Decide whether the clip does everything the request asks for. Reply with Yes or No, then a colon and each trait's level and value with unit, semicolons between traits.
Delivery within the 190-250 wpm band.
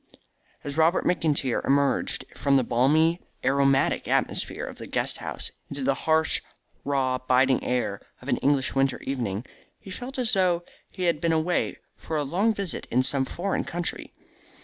No: average, 165 wpm